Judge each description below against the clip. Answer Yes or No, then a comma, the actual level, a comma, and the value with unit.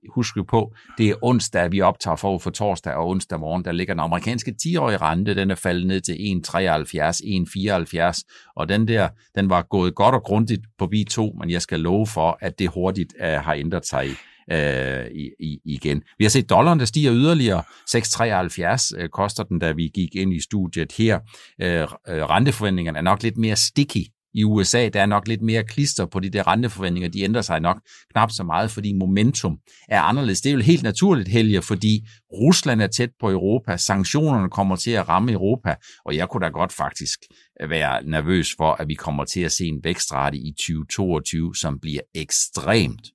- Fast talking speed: No, average, 195 wpm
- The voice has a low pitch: Yes, low, 100 Hz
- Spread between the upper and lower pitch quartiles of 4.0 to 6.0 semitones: Yes, average, 4.7 semitones